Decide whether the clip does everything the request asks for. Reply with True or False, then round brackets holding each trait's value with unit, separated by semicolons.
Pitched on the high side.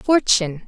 True (210 Hz)